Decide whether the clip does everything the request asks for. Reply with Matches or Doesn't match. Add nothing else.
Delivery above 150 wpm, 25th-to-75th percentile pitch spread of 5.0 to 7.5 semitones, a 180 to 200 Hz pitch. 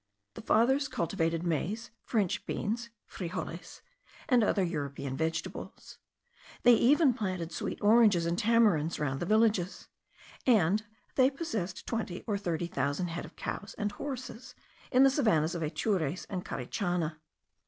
Doesn't match